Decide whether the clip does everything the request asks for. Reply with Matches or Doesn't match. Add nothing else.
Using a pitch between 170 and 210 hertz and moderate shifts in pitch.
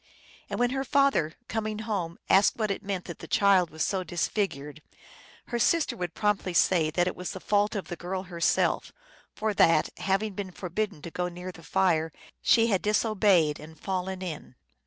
Matches